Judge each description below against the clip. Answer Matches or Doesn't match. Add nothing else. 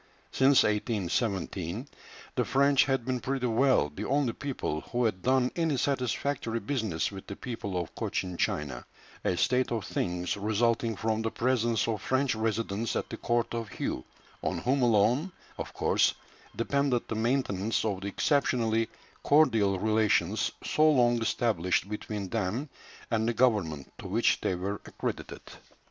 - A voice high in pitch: Doesn't match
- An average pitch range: Matches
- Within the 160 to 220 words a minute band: Doesn't match